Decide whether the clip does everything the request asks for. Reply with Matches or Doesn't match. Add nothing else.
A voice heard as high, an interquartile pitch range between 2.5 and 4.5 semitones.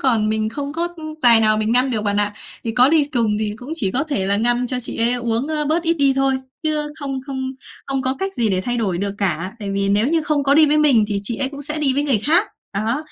Doesn't match